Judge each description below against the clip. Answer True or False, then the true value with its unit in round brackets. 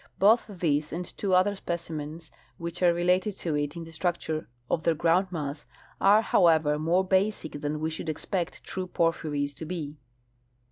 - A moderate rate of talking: True (160 wpm)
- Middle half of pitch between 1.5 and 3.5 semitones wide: True (3.0 semitones)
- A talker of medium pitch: True (170 Hz)